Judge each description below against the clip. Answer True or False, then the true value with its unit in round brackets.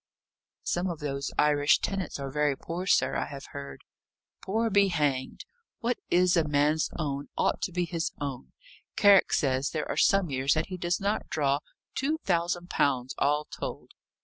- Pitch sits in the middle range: True (155 Hz)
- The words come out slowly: False (175 wpm)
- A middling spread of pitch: True (4.3 semitones)